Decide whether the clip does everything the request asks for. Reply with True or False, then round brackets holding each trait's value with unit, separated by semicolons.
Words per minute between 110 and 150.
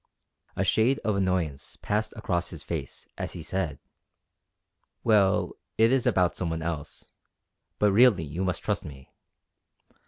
True (145 wpm)